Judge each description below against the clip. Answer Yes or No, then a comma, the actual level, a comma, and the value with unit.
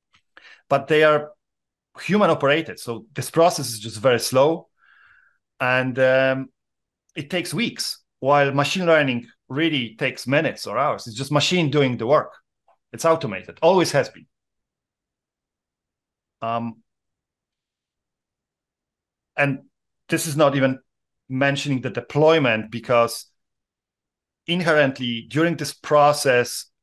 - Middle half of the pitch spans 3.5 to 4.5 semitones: Yes, average, 3.9 semitones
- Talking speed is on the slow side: Yes, slow, 110 wpm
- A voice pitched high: No, medium, 140 Hz